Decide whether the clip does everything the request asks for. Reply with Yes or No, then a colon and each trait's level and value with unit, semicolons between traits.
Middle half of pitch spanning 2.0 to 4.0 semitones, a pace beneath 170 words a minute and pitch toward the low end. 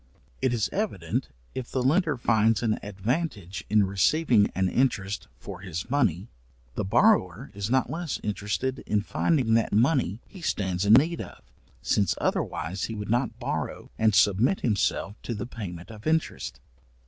No: average, 4.8 semitones; average, 160 wpm; low, 110 Hz